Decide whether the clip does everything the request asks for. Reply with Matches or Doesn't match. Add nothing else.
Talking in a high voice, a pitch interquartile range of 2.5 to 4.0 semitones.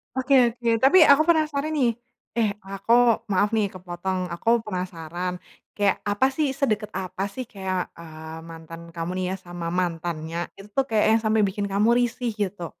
Doesn't match